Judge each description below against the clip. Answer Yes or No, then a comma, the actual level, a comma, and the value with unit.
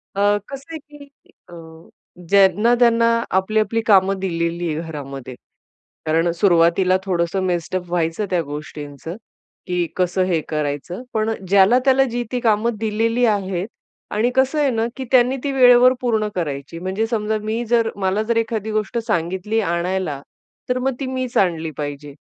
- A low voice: No, high, 195 Hz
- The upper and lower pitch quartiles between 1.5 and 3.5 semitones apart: No, average, 5.3 semitones